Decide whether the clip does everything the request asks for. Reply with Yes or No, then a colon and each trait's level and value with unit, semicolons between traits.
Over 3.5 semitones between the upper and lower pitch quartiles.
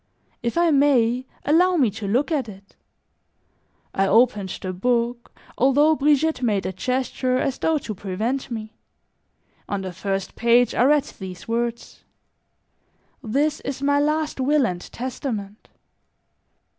Yes: average, 5.2 semitones